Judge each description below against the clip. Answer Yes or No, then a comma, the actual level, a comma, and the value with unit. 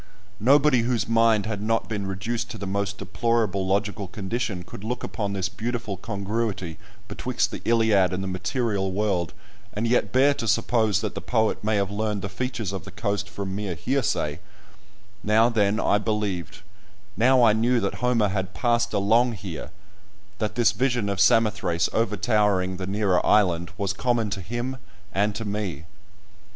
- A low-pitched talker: Yes, low, 105 Hz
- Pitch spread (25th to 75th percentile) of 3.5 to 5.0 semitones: No, average, 2.9 semitones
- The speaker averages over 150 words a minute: Yes, average, 170 wpm